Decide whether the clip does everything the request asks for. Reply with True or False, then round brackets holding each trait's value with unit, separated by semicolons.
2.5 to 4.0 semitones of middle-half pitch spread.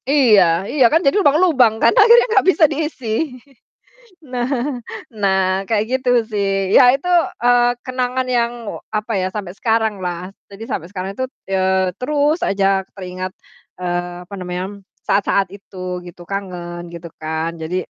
False (5.6 semitones)